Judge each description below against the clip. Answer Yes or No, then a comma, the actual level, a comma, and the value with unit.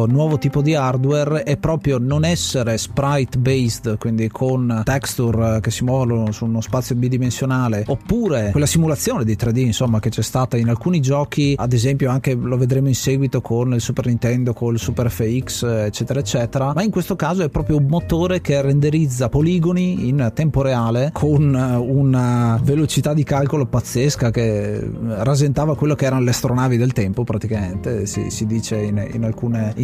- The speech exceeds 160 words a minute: Yes, fast, 170 wpm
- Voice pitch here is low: Yes, low, 130 Hz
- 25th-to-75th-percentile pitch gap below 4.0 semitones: Yes, average, 3.5 semitones